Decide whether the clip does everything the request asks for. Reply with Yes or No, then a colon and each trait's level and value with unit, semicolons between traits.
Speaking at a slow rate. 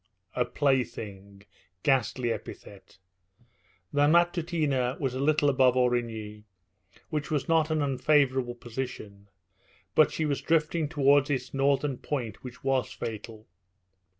Yes: slow, 120 wpm